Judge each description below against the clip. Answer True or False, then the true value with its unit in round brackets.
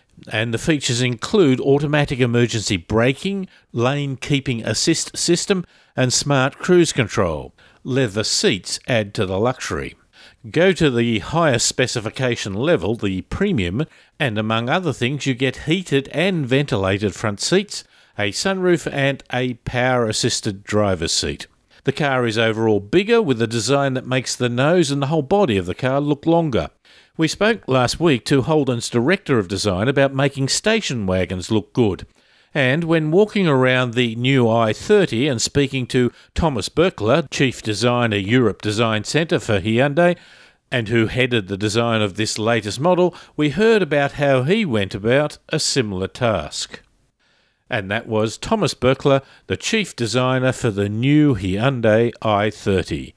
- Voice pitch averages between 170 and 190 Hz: False (130 Hz)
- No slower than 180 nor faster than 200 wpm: False (150 wpm)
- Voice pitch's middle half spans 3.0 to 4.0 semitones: False (4.8 semitones)